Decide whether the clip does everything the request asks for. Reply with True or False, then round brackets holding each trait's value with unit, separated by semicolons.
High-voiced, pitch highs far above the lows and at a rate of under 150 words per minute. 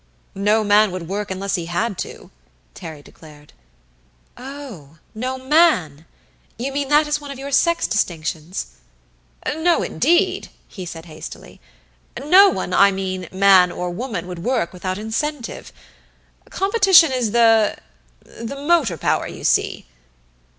True (215 Hz; 7.6 semitones; 135 wpm)